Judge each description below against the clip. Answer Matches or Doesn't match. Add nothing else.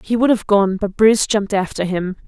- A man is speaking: Doesn't match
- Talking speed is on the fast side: Matches